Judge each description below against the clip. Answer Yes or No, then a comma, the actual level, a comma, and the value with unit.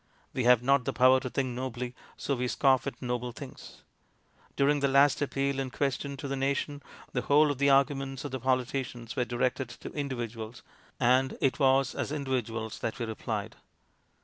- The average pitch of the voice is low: Yes, low, 130 Hz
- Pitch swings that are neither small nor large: No, narrow, 2.0 semitones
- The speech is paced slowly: No, average, 180 wpm